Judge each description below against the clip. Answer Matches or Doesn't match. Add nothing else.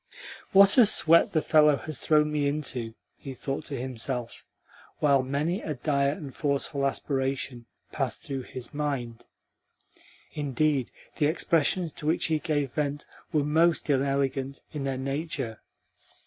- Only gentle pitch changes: Matches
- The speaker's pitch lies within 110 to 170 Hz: Matches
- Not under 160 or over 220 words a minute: Doesn't match